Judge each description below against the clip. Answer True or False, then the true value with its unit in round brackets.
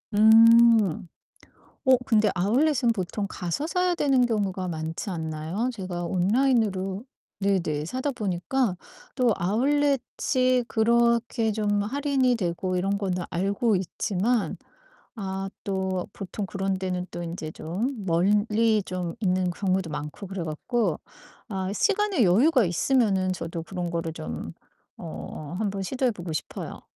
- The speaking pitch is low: False (195 Hz)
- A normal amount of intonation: True (4.7 semitones)